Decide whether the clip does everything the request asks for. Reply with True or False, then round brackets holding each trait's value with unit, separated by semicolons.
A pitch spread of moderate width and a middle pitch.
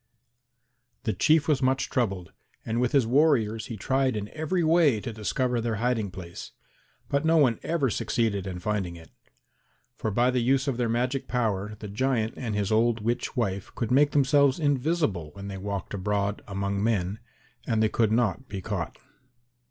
False (4.5 semitones; 115 Hz)